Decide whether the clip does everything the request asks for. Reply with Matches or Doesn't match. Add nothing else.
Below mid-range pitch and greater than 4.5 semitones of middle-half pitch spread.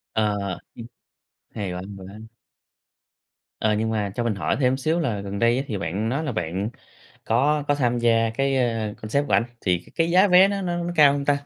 Matches